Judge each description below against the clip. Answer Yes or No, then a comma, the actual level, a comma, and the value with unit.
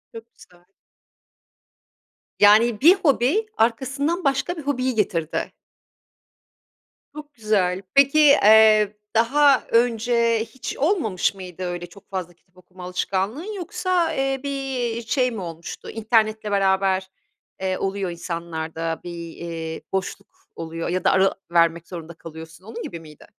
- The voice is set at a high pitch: Yes, high, 210 Hz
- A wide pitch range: Yes, wide, 6.6 semitones